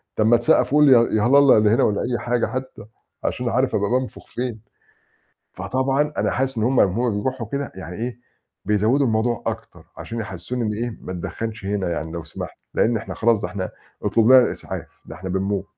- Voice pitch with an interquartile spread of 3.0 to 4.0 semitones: Yes, average, 3.7 semitones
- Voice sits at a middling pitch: No, low, 115 Hz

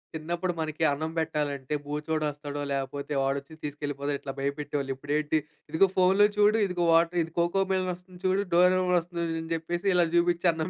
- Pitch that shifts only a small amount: No, average, 3.6 semitones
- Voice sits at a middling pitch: Yes, medium, 160 Hz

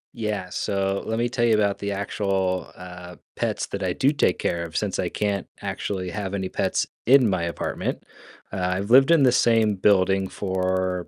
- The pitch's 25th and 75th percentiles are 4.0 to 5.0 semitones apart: No, average, 2.8 semitones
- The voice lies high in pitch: No, low, 100 Hz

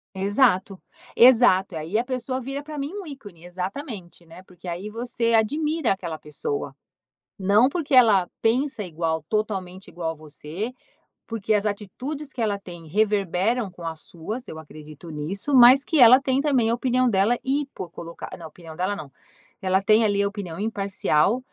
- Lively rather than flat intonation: Yes, wide, 6.0 semitones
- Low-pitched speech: No, high, 205 Hz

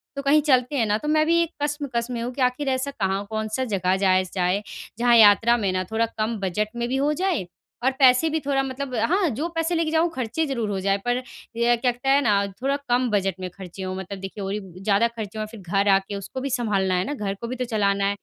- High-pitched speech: Yes, high, 235 Hz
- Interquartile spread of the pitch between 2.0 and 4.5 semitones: No, average, 5.3 semitones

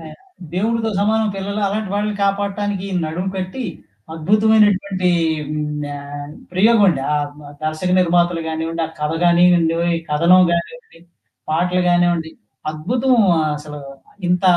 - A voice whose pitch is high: No, medium, 180 Hz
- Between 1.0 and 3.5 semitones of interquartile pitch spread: No, average, 4.2 semitones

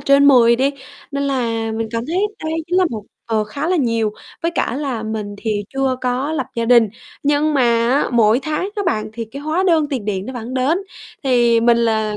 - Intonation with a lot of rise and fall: No, average, 4.2 semitones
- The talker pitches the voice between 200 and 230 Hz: No, very high, 250 Hz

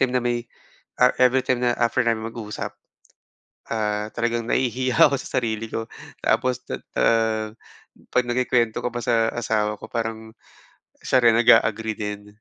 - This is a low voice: Yes, low, 115 Hz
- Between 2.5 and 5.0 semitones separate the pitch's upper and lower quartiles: No, narrow, 1.8 semitones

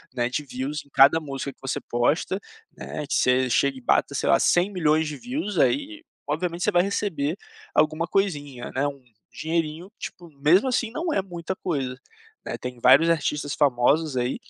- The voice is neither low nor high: Yes, medium, 155 Hz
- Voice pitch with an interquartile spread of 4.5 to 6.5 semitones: Yes, average, 4.9 semitones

